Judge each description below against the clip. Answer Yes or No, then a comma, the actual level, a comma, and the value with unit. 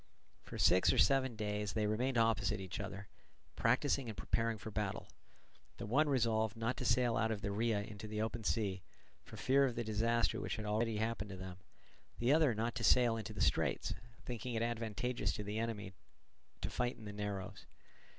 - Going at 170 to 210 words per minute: Yes, average, 200 wpm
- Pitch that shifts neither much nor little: No, narrow, 2.2 semitones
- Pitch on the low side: Yes, low, 110 Hz